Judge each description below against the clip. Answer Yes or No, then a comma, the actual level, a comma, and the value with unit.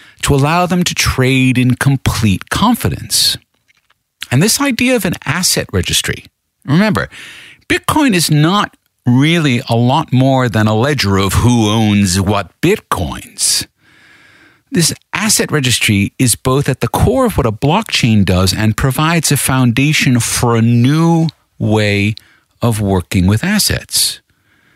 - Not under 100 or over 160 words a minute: Yes, slow, 135 wpm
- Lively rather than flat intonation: Yes, wide, 6.0 semitones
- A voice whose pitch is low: Yes, low, 125 Hz